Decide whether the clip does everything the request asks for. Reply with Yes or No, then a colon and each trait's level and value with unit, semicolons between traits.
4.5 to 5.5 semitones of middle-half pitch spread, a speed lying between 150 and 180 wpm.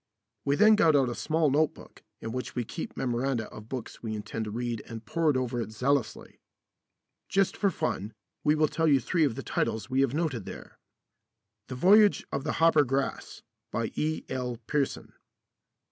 Yes: average, 4.8 semitones; average, 175 wpm